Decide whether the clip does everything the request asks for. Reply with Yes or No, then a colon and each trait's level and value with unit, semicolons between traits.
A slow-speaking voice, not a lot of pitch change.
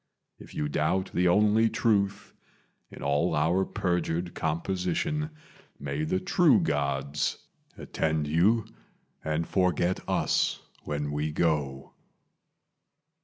No: slow, 105 wpm; average, 4.4 semitones